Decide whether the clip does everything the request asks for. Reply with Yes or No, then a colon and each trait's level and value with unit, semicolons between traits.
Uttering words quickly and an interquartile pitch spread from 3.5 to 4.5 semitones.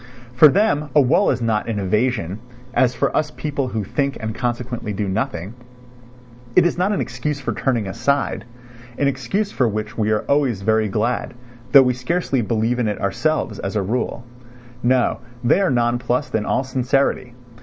No: average, 175 wpm; average, 4.1 semitones